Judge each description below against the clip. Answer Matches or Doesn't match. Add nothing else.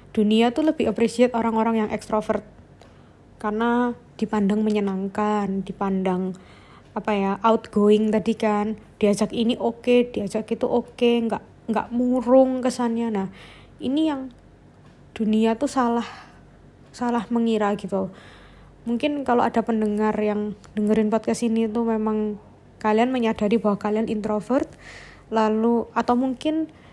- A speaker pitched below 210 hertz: Doesn't match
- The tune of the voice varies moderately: Doesn't match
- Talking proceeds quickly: Doesn't match